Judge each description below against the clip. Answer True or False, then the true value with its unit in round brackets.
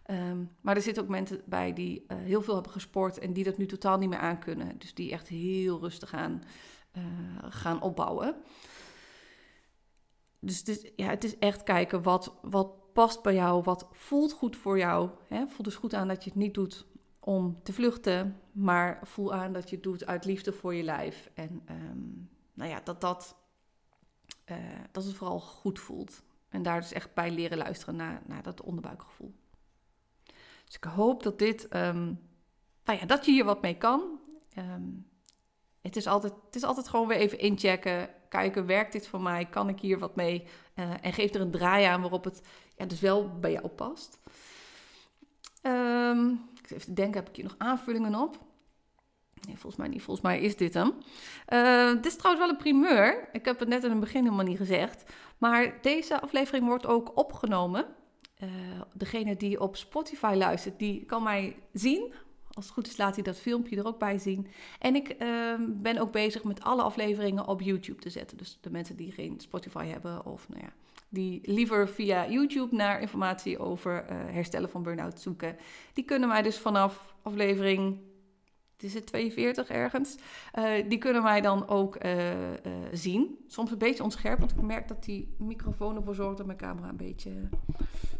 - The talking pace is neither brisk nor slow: True (190 wpm)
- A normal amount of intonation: True (4.0 semitones)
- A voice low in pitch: False (200 Hz)